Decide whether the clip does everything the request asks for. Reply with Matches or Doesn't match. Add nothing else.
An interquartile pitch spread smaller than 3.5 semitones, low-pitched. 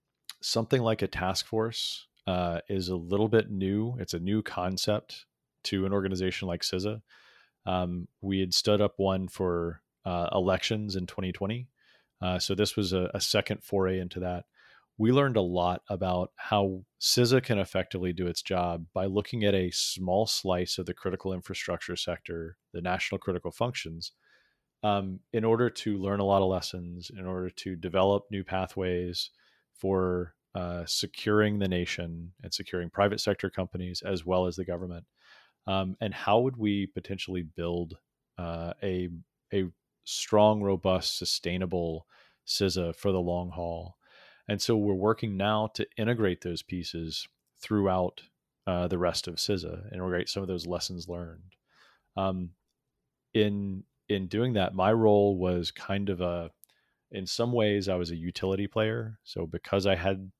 Matches